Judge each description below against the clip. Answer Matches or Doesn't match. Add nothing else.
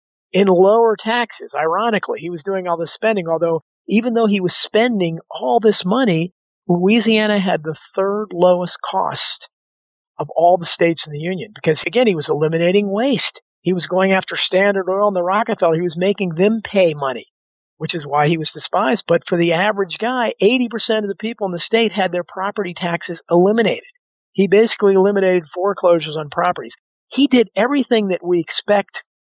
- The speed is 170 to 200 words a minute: Matches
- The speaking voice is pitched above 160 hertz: Matches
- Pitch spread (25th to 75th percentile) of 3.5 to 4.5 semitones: Matches